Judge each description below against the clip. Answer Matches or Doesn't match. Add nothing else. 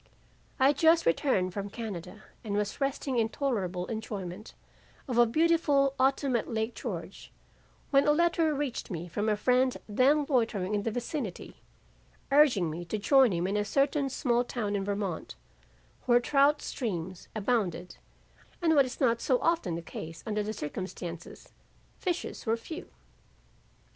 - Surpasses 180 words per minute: Doesn't match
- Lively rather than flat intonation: Matches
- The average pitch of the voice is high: Matches